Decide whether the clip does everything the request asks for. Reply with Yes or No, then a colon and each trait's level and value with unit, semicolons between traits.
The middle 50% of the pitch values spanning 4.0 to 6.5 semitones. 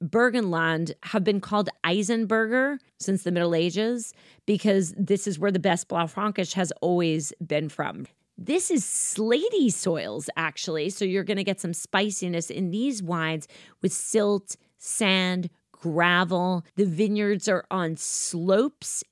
No: average, 3.4 semitones